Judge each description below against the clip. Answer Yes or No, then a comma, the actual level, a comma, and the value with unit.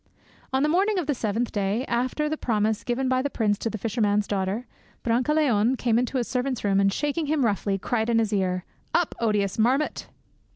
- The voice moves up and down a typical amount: Yes, average, 4.4 semitones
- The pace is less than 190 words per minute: No, average, 200 wpm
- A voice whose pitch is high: Yes, high, 235 Hz